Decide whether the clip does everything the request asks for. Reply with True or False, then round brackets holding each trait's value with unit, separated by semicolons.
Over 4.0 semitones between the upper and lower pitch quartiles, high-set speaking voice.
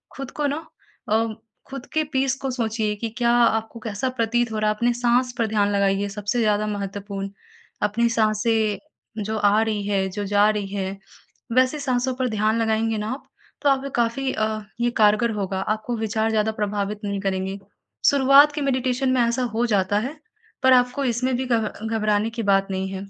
False (3.2 semitones; 220 Hz)